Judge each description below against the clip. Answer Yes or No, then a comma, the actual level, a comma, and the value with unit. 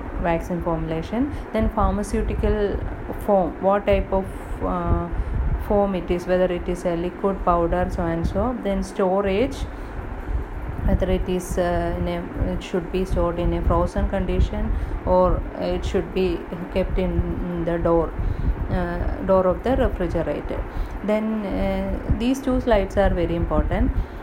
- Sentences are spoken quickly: No, average, 145 wpm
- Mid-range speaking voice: Yes, medium, 180 Hz